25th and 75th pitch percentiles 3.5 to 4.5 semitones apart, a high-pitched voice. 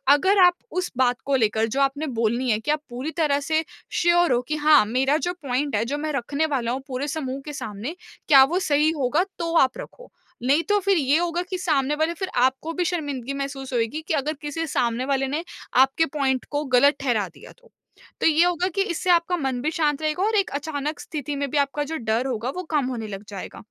Yes: average, 3.8 semitones; very high, 285 Hz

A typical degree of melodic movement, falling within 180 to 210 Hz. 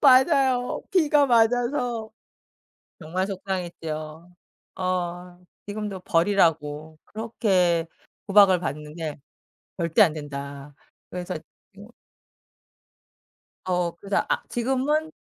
No: wide, 6.0 semitones; medium, 185 Hz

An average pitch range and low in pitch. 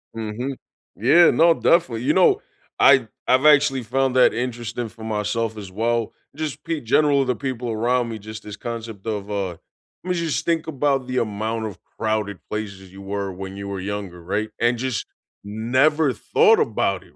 Yes: average, 4.3 semitones; low, 115 Hz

